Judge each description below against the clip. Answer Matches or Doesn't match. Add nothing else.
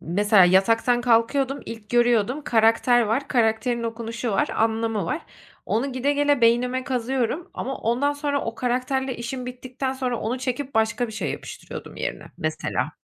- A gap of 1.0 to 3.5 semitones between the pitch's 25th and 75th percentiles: Matches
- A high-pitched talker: Matches